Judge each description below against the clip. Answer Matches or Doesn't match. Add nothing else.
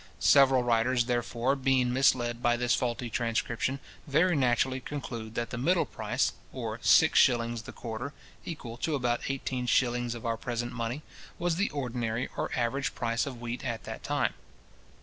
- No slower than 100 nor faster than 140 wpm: Doesn't match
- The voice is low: Matches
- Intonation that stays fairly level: Matches